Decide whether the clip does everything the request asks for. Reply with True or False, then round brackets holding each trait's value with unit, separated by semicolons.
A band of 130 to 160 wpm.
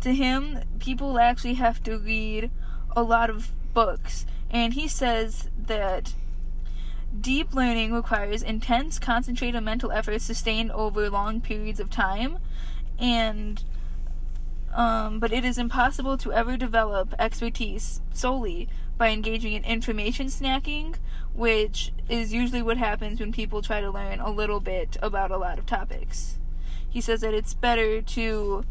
True (140 wpm)